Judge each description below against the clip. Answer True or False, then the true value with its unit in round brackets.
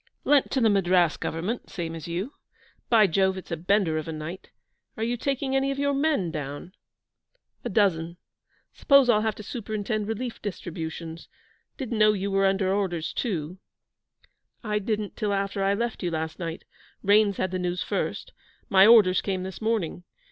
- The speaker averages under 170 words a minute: False (175 wpm)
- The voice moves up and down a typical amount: True (4.1 semitones)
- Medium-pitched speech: False (195 Hz)